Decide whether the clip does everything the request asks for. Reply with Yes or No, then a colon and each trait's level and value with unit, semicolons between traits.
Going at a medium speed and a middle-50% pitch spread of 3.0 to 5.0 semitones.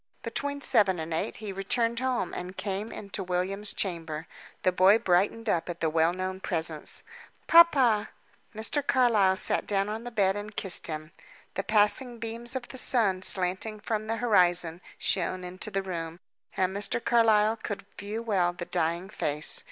Yes: average, 165 wpm; average, 3.8 semitones